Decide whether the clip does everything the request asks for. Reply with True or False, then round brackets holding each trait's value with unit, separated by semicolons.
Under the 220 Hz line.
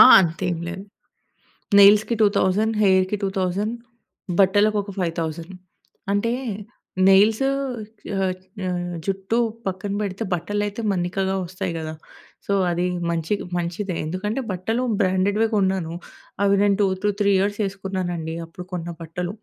True (190 Hz)